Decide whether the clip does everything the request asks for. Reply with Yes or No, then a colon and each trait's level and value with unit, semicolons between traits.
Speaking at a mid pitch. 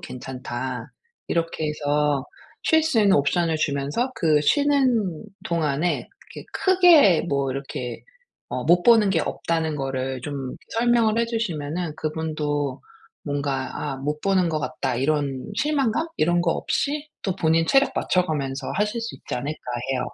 Yes: medium, 160 Hz